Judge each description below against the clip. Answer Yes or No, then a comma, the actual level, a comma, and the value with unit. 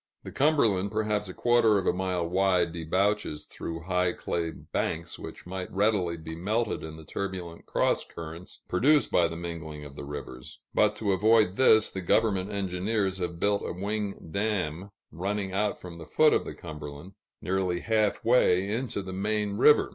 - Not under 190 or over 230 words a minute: No, average, 175 wpm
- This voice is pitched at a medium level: No, very low, 95 Hz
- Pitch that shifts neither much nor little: Yes, average, 3.7 semitones